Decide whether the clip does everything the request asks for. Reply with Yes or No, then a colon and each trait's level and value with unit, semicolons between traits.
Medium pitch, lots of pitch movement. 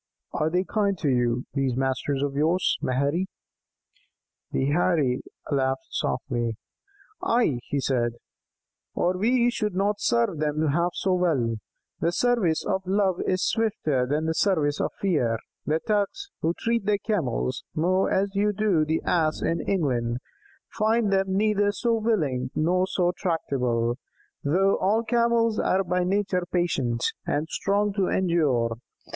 Yes: medium, 175 Hz; wide, 6.2 semitones